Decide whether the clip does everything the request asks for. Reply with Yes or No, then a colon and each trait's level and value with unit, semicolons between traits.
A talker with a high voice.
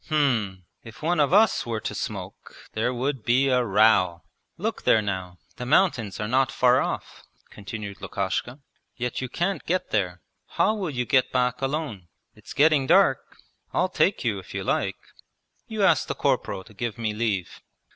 No: low, 125 Hz